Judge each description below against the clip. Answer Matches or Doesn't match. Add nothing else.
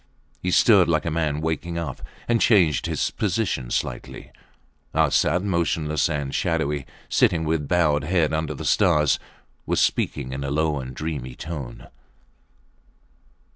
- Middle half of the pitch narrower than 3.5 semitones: Matches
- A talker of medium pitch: Doesn't match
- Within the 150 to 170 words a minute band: Doesn't match